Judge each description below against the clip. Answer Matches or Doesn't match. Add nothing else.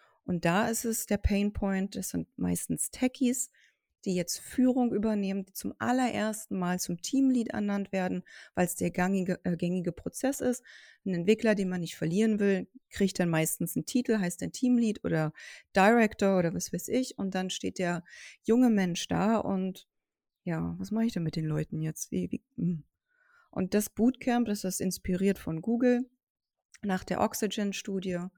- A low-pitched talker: Doesn't match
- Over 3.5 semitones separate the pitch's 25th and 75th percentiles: Matches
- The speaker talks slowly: Doesn't match